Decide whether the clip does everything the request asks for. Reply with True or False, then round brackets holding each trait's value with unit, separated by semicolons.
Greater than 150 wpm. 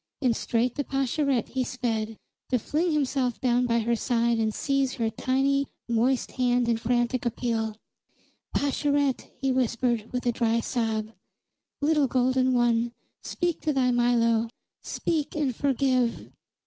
False (140 wpm)